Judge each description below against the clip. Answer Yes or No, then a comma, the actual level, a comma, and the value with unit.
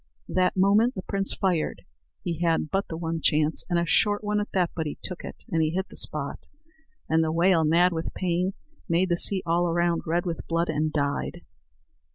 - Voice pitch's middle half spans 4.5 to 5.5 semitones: No, narrow, 2.4 semitones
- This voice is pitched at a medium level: Yes, medium, 170 Hz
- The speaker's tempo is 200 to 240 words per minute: Yes, fast, 205 wpm